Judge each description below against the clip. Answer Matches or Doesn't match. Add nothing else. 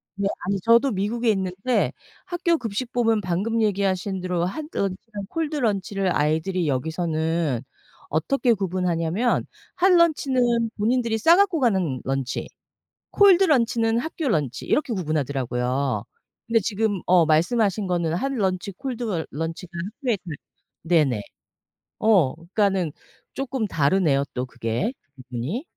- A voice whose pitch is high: Matches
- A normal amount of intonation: Doesn't match